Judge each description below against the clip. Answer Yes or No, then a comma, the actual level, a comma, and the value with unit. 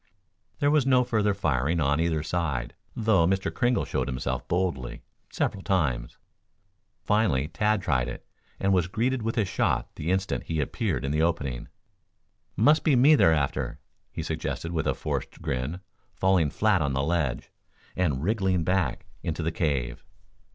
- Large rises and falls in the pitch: Yes, wide, 6.1 semitones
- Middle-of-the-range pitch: No, very low, 85 Hz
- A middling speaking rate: Yes, average, 160 wpm